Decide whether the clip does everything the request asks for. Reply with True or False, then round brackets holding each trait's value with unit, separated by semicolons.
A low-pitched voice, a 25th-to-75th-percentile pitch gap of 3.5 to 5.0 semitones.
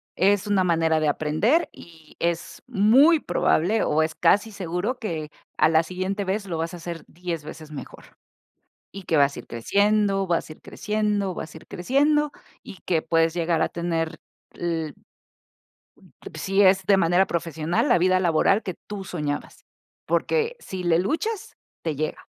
False (175 Hz; 3.9 semitones)